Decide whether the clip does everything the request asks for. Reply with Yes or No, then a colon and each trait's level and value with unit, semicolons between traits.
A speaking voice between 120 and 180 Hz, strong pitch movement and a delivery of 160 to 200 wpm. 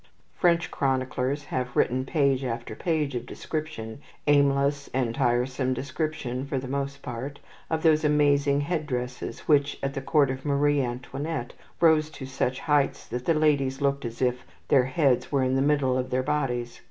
No: medium, 140 Hz; narrow, 2.4 semitones; average, 170 wpm